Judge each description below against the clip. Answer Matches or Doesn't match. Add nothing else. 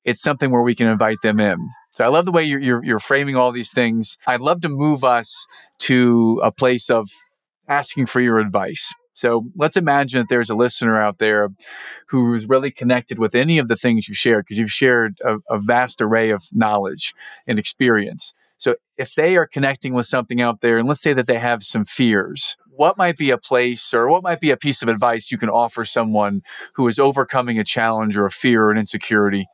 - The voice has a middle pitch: Doesn't match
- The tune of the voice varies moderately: Matches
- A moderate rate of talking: Doesn't match